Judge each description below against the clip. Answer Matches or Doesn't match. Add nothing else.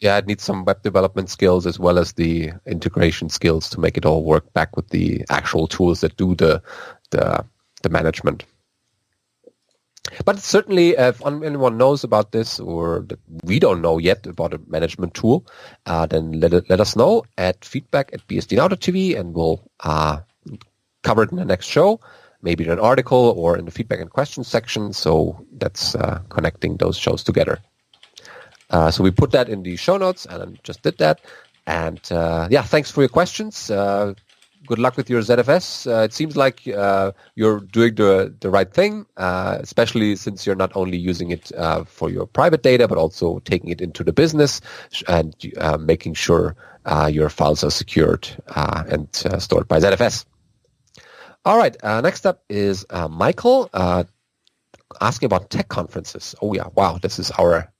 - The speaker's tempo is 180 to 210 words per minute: Matches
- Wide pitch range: Matches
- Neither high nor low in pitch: Doesn't match